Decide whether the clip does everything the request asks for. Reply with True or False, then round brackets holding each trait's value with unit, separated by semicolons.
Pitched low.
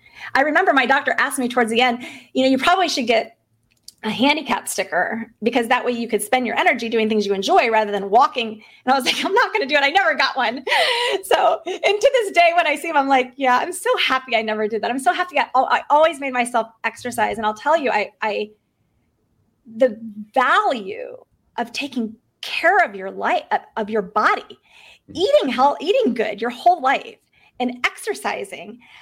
False (255 Hz)